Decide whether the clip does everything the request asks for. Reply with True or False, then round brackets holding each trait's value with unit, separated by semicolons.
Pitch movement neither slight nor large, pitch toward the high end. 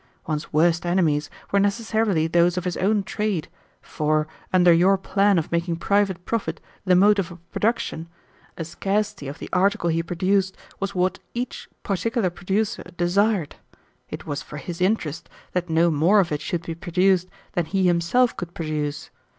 False (3.1 semitones; 180 Hz)